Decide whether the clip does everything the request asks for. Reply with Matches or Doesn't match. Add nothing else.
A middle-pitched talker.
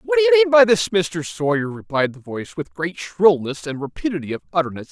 Matches